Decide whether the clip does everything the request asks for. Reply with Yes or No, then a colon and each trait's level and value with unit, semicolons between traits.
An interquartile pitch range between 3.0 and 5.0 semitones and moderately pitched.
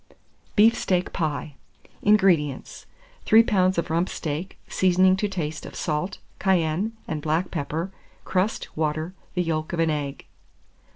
Yes: average, 3.3 semitones; medium, 170 Hz